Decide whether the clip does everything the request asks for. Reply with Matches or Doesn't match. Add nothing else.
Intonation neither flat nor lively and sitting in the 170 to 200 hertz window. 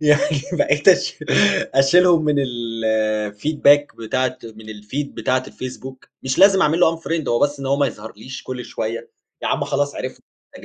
Doesn't match